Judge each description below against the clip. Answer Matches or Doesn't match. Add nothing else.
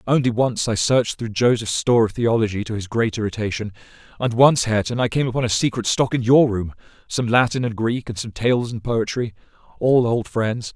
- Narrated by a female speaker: Doesn't match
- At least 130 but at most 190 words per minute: Doesn't match